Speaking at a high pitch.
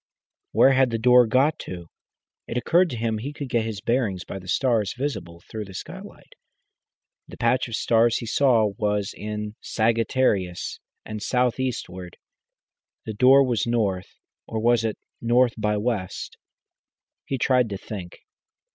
No: low, 115 Hz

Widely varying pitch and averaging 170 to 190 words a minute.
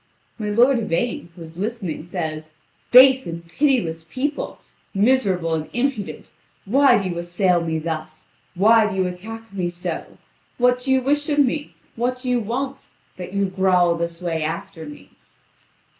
No: wide, 6.7 semitones; average, 160 wpm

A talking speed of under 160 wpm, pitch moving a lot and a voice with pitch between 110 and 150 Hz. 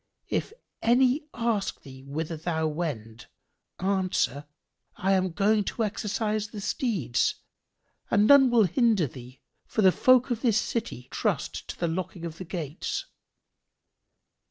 No: average, 140 wpm; wide, 6.0 semitones; high, 190 Hz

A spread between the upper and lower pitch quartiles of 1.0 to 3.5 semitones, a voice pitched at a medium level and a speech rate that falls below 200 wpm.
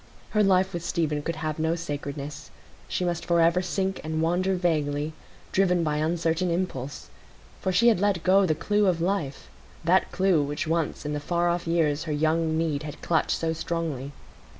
Yes: average, 2.7 semitones; medium, 165 Hz; average, 175 wpm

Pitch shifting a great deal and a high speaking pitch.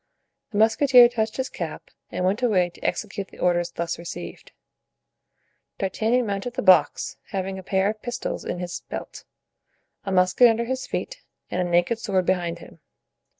No: average, 4.6 semitones; high, 195 Hz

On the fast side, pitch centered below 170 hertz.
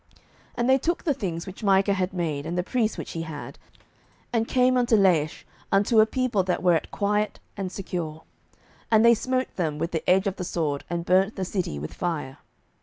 No: fast, 210 wpm; high, 190 Hz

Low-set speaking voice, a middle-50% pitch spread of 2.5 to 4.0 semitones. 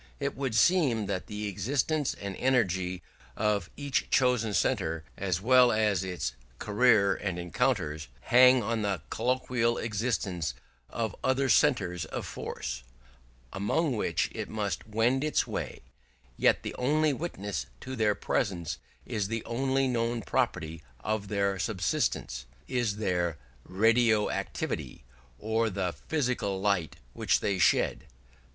No: low, 110 Hz; average, 4.7 semitones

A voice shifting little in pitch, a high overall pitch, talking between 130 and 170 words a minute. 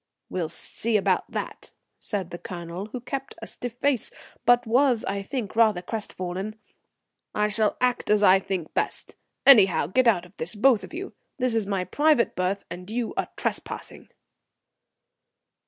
No: average, 4.7 semitones; high, 210 Hz; average, 160 wpm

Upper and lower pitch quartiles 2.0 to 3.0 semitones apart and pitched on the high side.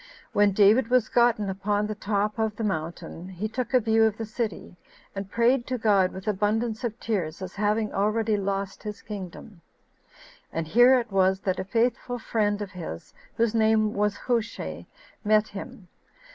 Yes: narrow, 2.4 semitones; high, 210 Hz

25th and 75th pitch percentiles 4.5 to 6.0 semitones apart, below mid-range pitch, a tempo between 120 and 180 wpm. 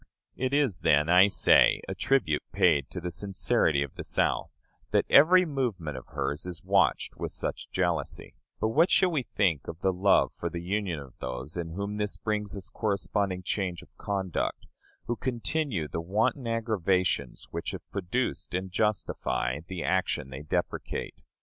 Yes: average, 4.9 semitones; very low, 95 Hz; average, 170 wpm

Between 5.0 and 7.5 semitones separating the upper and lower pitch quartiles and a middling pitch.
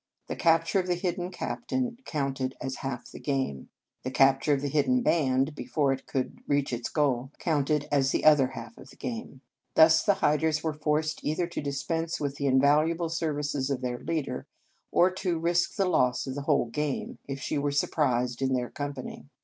No: average, 3.3 semitones; medium, 145 Hz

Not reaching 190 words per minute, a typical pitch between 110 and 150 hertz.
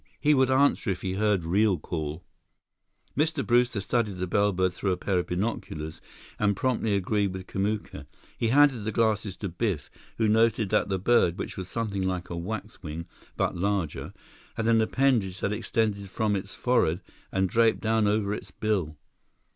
No: average, 170 wpm; low, 100 Hz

